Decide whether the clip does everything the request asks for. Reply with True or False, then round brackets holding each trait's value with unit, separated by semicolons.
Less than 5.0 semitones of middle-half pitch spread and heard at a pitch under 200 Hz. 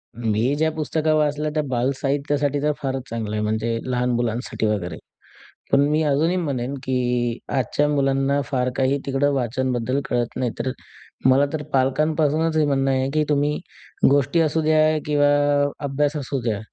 True (3.0 semitones; 135 Hz)